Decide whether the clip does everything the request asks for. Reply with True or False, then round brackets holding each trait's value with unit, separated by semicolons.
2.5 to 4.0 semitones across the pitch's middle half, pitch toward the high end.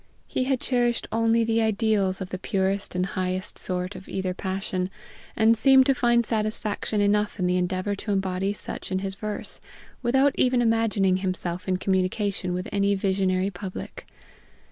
True (3.3 semitones; 200 Hz)